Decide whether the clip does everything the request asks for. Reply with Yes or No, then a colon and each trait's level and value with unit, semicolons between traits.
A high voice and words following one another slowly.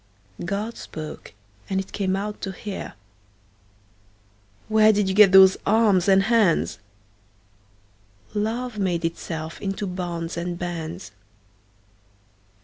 No: medium, 170 Hz; slow, 100 wpm